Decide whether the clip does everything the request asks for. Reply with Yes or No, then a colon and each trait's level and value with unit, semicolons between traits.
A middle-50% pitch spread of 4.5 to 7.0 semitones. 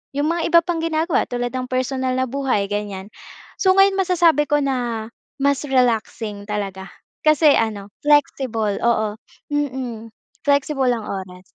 Yes: average, 5.2 semitones